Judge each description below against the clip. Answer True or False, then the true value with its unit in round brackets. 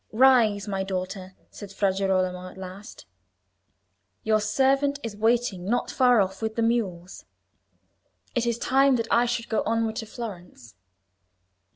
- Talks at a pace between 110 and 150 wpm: True (145 wpm)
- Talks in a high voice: True (215 Hz)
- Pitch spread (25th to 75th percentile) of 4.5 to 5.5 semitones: False (3.8 semitones)